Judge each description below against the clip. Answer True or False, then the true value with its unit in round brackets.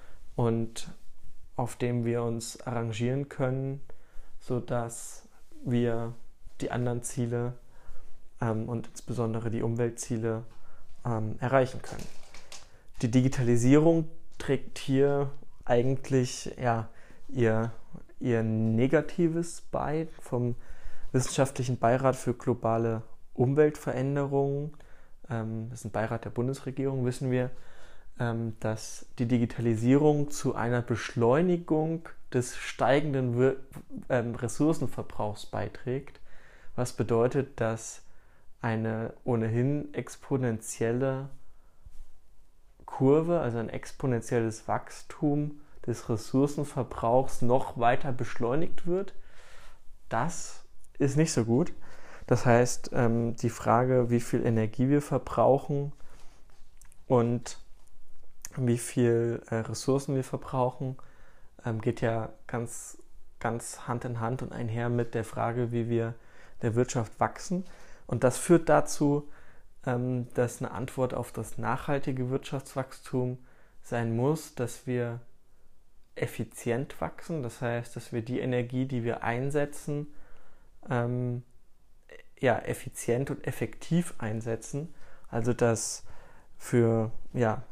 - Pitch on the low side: True (120 Hz)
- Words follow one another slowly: True (100 wpm)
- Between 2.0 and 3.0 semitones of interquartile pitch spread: True (2.7 semitones)